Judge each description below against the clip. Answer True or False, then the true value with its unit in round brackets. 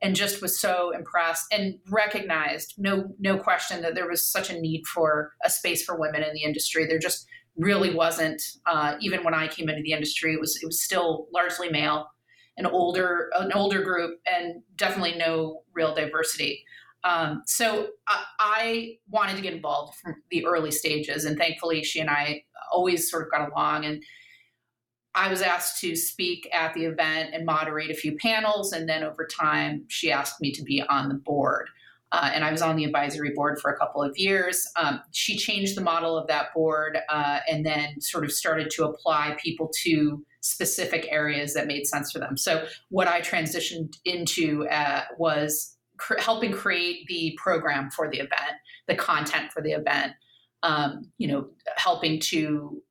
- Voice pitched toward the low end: False (165 Hz)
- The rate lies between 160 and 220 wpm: True (185 wpm)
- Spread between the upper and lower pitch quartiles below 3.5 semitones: True (2.8 semitones)